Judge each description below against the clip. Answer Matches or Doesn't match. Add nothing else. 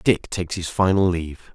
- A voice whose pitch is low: Matches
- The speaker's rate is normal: Matches